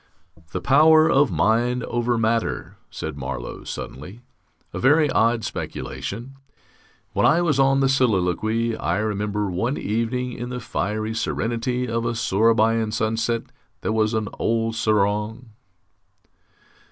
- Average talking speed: No, slow, 130 wpm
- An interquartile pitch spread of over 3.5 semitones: No, narrow, 2.5 semitones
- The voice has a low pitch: Yes, low, 115 Hz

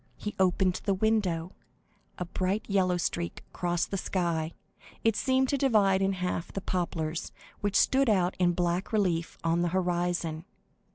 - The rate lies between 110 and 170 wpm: Yes, average, 155 wpm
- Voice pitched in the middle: Yes, medium, 180 Hz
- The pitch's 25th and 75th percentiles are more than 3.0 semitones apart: No, narrow, 2.5 semitones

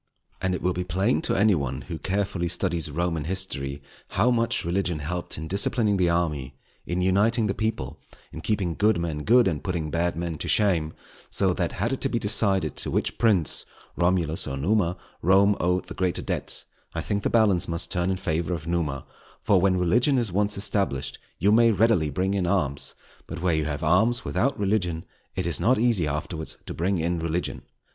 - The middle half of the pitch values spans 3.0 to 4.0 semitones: Yes, average, 3.7 semitones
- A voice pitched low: Yes, very low, 90 Hz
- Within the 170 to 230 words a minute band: Yes, average, 200 wpm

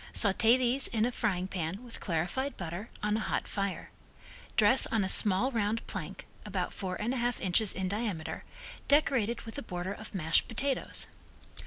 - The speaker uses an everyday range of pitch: Yes, average, 4.2 semitones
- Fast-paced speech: No, average, 175 wpm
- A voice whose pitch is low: No, high, 210 Hz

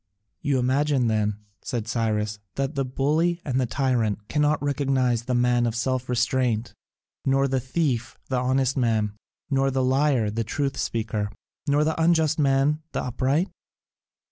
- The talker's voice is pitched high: No, low, 130 Hz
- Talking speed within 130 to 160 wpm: Yes, average, 150 wpm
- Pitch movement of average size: Yes, average, 3.2 semitones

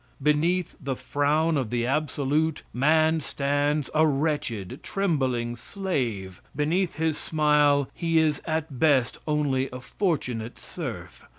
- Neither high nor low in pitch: Yes, medium, 150 Hz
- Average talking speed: No, slow, 120 wpm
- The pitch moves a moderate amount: Yes, average, 3.3 semitones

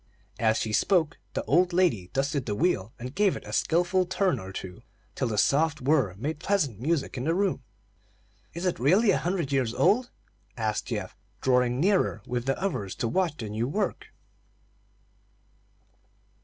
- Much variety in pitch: Yes, wide, 7.5 semitones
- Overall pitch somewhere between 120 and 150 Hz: Yes, medium, 140 Hz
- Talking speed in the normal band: Yes, average, 170 wpm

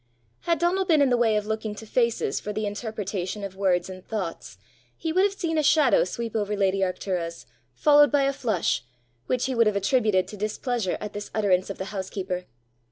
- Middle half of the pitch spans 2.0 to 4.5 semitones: No, average, 4.9 semitones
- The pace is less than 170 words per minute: No, fast, 205 wpm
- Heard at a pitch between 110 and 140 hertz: No, high, 210 Hz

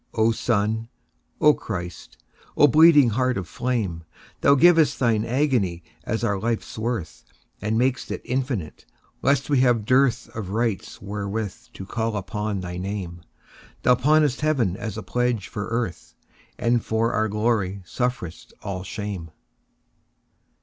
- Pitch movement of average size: Yes, average, 4.2 semitones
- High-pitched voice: No, low, 110 Hz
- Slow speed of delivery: Yes, slow, 125 wpm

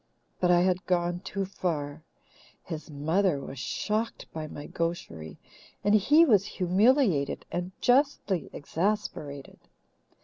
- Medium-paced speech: No, slow, 115 wpm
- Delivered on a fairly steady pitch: No, average, 4.8 semitones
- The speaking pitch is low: No, medium, 180 Hz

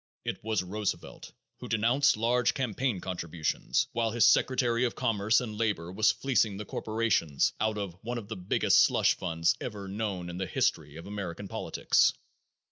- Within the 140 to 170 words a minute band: Yes, average, 165 wpm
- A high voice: No, low, 105 Hz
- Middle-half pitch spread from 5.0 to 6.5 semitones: No, average, 3.7 semitones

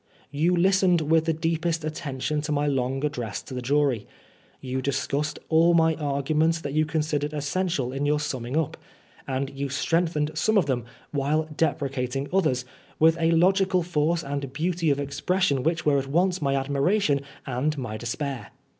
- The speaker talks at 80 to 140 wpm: No, average, 165 wpm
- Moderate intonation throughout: Yes, average, 3.0 semitones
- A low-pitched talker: No, medium, 150 Hz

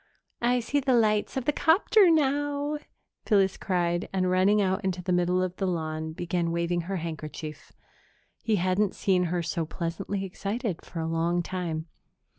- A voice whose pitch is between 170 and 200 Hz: Yes, medium, 185 Hz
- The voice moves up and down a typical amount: Yes, average, 3.8 semitones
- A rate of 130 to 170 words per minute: Yes, average, 165 wpm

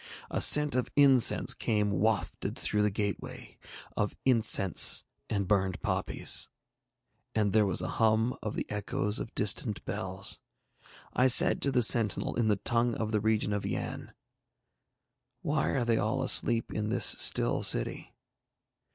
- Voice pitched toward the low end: Yes, low, 110 Hz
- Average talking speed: Yes, average, 150 wpm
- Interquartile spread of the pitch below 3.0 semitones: Yes, narrow, 2.5 semitones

